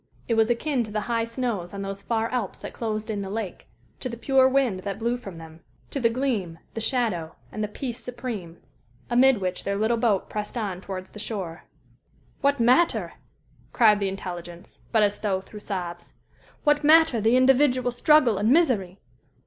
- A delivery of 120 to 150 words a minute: No, average, 185 wpm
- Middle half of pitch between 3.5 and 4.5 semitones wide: Yes, average, 4.1 semitones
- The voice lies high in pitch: Yes, high, 220 Hz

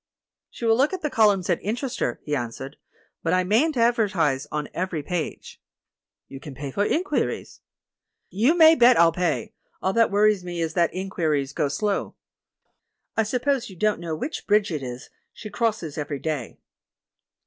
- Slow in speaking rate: No, average, 170 wpm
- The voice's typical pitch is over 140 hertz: Yes, medium, 185 Hz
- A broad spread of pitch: Yes, wide, 6.9 semitones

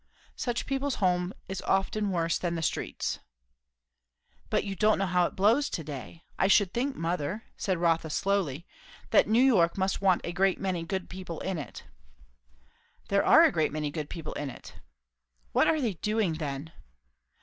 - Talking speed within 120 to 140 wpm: No, average, 170 wpm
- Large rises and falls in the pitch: No, average, 3.5 semitones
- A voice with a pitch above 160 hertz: Yes, medium, 185 Hz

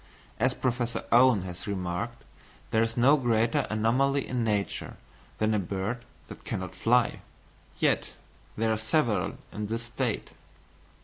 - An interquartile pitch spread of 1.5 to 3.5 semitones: Yes, narrow, 2.6 semitones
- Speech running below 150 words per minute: Yes, slow, 135 wpm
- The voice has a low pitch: Yes, low, 115 Hz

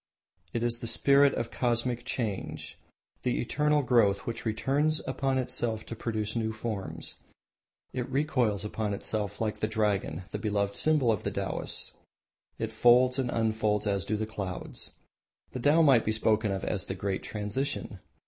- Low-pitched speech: Yes, low, 110 Hz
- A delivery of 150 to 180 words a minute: Yes, average, 160 wpm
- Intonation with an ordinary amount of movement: Yes, average, 3.2 semitones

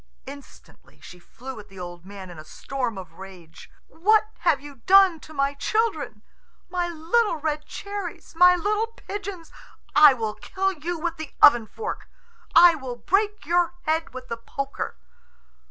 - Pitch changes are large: Yes, wide, 7.4 semitones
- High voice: Yes, very high, 310 Hz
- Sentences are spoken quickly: No, average, 160 wpm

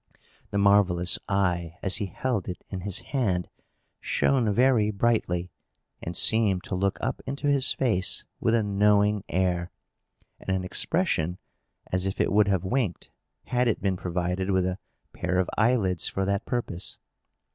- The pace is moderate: Yes, average, 155 wpm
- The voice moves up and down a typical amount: Yes, average, 3.5 semitones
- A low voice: Yes, low, 100 Hz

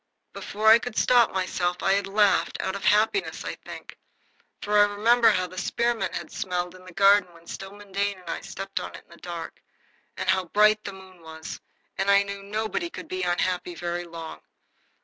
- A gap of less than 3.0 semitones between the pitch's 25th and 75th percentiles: Yes, narrow, 2.6 semitones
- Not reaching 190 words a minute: No, average, 200 wpm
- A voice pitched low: No, high, 195 Hz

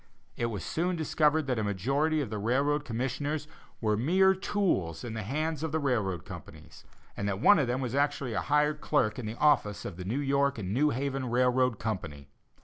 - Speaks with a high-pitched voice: No, low, 130 Hz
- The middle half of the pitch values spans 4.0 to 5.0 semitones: No, wide, 5.6 semitones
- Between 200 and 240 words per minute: Yes, fast, 205 wpm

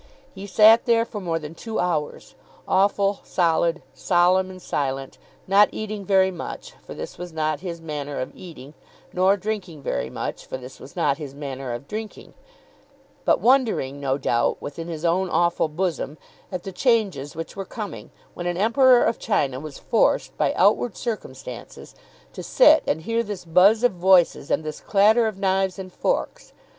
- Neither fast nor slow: Yes, average, 170 wpm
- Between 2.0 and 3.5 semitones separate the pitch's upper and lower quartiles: No, average, 5.2 semitones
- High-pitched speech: No, medium, 180 Hz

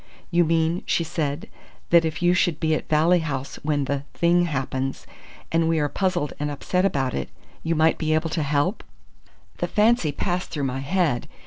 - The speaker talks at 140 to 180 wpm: No, average, 190 wpm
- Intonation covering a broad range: No, average, 3.2 semitones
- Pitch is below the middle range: No, medium, 160 Hz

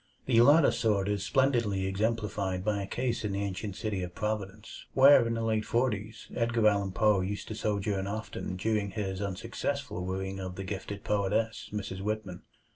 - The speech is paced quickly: No, average, 175 wpm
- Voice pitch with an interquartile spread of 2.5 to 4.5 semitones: Yes, average, 2.8 semitones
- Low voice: Yes, low, 105 Hz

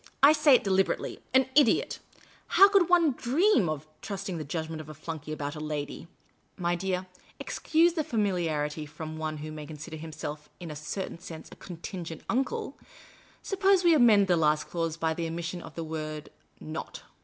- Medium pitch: Yes, medium, 165 Hz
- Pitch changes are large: Yes, wide, 6.3 semitones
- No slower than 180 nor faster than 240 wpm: Yes, average, 190 wpm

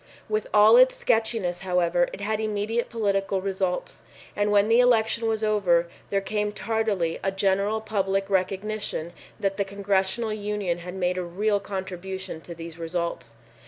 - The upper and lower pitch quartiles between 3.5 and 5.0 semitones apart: No, average, 2.8 semitones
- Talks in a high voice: Yes, high, 195 Hz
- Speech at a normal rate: Yes, average, 155 wpm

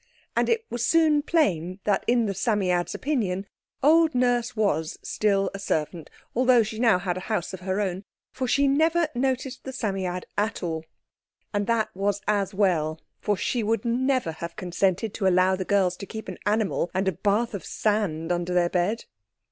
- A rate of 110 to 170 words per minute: No, average, 185 wpm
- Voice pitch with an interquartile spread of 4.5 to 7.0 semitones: Yes, average, 4.9 semitones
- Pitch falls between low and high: No, high, 205 Hz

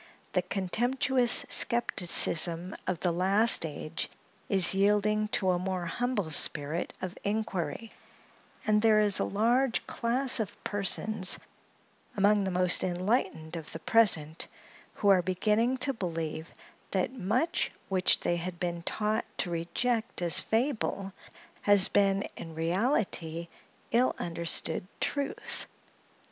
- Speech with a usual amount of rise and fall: Yes, average, 4.1 semitones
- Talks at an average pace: No, slow, 125 wpm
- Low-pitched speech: No, high, 195 Hz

